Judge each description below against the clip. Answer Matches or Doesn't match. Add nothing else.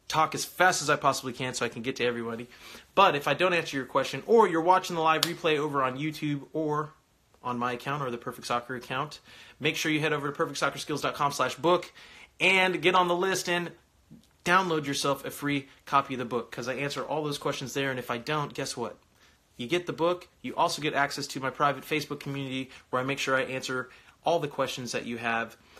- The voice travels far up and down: Doesn't match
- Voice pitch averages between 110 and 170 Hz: Matches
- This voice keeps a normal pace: Doesn't match